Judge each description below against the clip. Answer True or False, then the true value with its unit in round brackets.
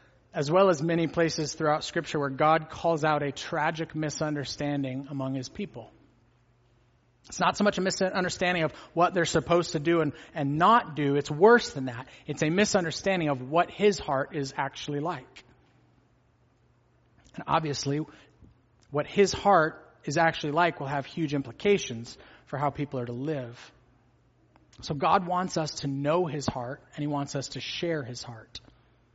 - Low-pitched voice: False (150 Hz)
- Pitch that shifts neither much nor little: True (4.1 semitones)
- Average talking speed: True (165 wpm)